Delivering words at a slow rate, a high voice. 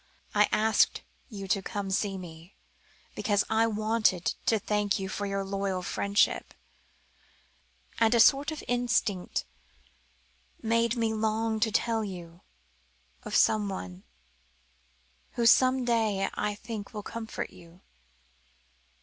Yes: slow, 125 wpm; high, 210 Hz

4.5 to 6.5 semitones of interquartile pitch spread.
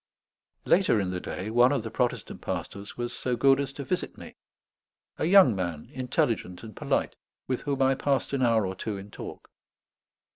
Yes: average, 5.0 semitones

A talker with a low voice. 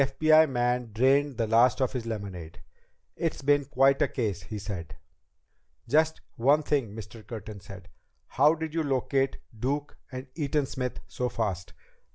Yes: low, 130 Hz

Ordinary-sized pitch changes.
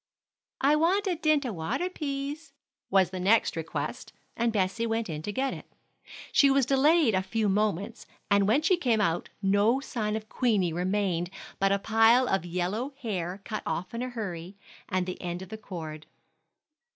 No: wide, 5.8 semitones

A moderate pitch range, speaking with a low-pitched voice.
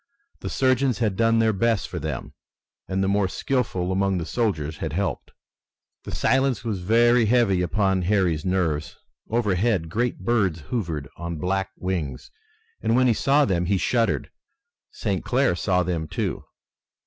Yes: average, 4.7 semitones; low, 100 Hz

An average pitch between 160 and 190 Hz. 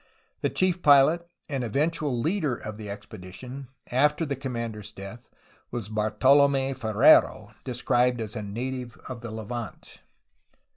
No: low, 120 Hz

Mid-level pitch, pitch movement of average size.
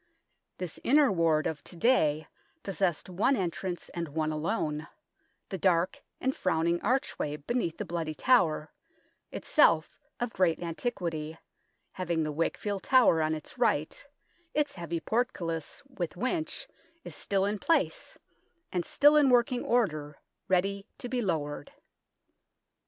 No: medium, 180 Hz; wide, 7.1 semitones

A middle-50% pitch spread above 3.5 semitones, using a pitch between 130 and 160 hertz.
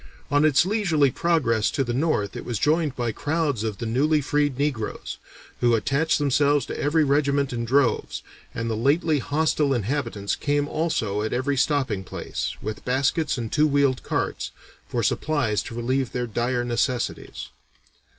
Yes: average, 3.9 semitones; low, 135 Hz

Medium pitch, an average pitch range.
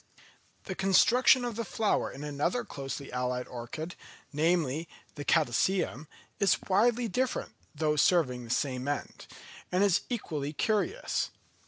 No: medium, 160 Hz; wide, 6.7 semitones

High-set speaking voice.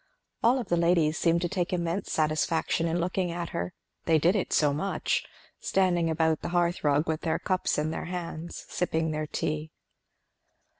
No: medium, 170 Hz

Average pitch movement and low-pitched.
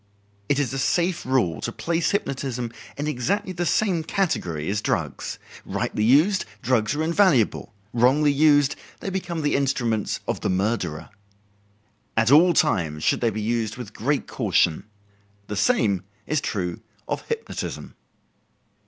No: wide, 6.6 semitones; low, 130 Hz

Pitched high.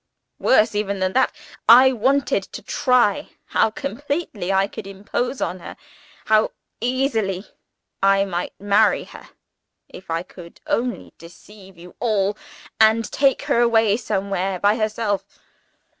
Yes: high, 210 Hz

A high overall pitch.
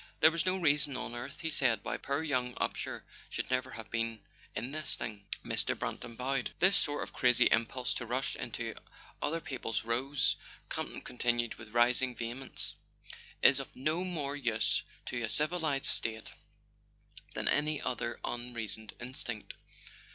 No: low, 125 Hz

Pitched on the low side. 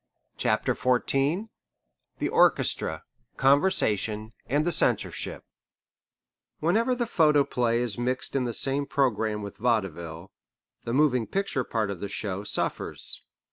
Yes: low, 125 Hz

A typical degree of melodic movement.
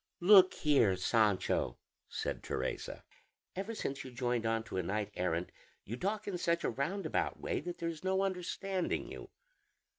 No: wide, 8.9 semitones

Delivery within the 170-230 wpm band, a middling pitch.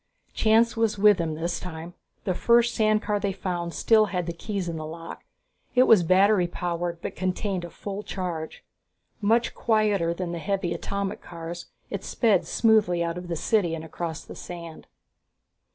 Yes: average, 175 wpm; medium, 180 Hz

